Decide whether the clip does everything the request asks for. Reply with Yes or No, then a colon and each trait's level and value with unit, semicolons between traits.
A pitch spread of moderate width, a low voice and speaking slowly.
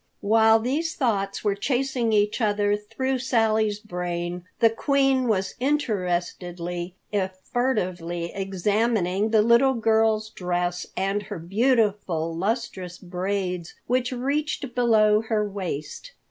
No: average, 4.6 semitones; high, 210 Hz; slow, 115 wpm